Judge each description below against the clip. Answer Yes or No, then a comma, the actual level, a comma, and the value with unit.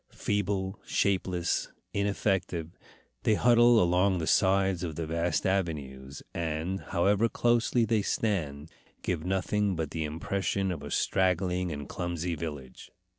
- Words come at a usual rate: No, slow, 125 wpm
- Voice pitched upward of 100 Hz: No, very low, 90 Hz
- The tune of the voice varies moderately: Yes, average, 3.4 semitones